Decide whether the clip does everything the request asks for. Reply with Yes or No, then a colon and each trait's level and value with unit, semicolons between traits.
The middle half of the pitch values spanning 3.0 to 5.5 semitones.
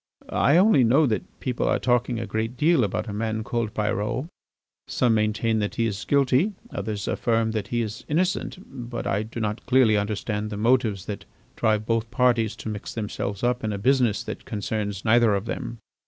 No: narrow, 2.6 semitones